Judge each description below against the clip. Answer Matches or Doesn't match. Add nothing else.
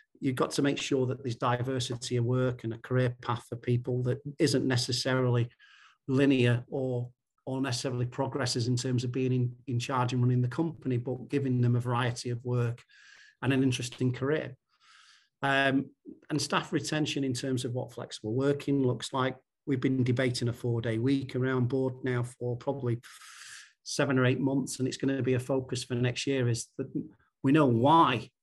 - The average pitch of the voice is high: Doesn't match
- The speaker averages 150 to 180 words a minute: Doesn't match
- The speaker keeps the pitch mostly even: Matches